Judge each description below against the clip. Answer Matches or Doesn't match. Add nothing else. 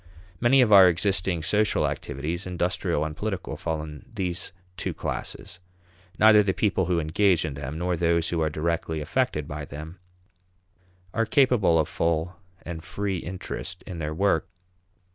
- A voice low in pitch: Matches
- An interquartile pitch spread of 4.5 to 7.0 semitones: Doesn't match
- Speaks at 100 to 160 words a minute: Matches